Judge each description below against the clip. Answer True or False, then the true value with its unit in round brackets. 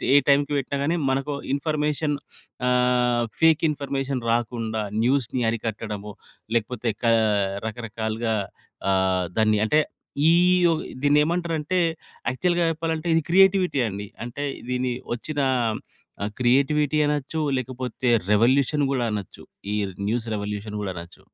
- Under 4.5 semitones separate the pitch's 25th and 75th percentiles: False (4.9 semitones)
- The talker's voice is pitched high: False (130 Hz)